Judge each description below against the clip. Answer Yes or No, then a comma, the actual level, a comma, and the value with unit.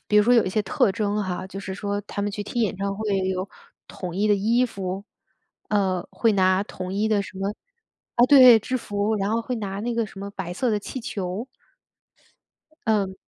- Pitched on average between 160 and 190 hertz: No, high, 205 Hz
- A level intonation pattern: Yes, narrow, 2.3 semitones